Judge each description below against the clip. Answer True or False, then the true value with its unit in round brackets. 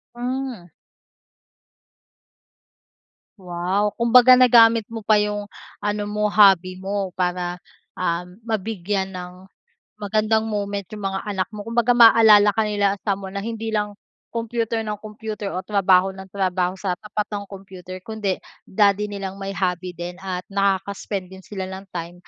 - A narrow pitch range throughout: True (2.3 semitones)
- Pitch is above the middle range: True (200 Hz)